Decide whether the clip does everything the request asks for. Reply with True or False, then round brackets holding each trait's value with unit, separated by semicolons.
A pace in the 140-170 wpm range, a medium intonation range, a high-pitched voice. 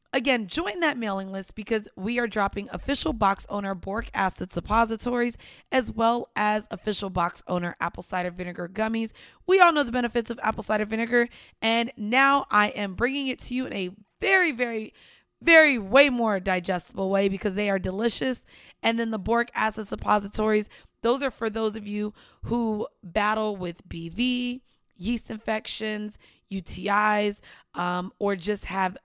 True (160 wpm; 3.3 semitones; 215 Hz)